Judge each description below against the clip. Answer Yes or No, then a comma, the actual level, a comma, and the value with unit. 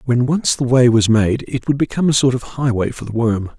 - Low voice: Yes, low, 125 Hz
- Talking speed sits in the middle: No, fast, 270 wpm